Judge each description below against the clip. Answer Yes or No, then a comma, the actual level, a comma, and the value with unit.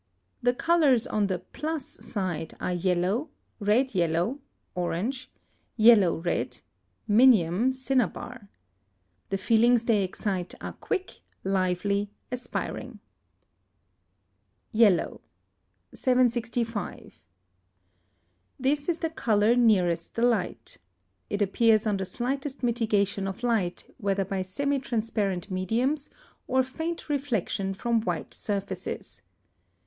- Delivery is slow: Yes, slow, 100 wpm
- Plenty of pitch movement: No, average, 4.8 semitones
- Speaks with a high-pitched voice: Yes, high, 220 Hz